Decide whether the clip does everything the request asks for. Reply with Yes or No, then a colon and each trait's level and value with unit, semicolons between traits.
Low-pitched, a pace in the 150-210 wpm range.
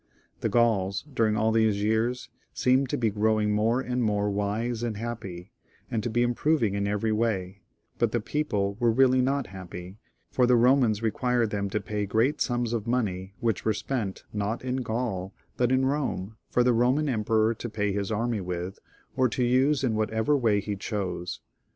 Yes: low, 110 Hz; average, 180 wpm